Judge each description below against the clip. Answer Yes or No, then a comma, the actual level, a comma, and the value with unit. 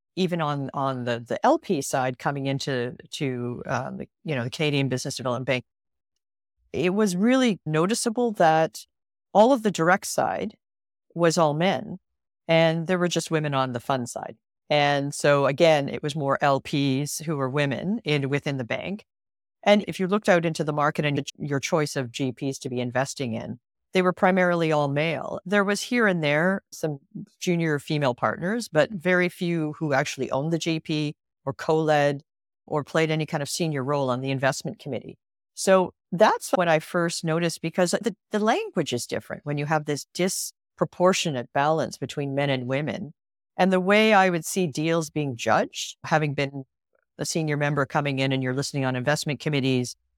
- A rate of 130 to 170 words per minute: No, average, 180 wpm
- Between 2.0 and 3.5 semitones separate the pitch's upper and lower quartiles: No, average, 4.6 semitones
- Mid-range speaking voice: Yes, medium, 155 Hz